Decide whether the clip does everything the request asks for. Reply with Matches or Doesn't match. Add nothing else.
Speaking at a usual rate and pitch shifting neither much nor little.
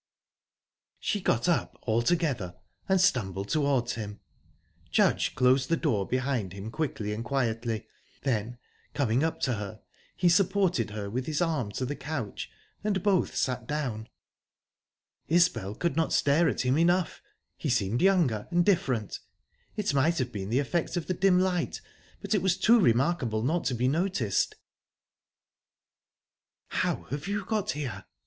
Doesn't match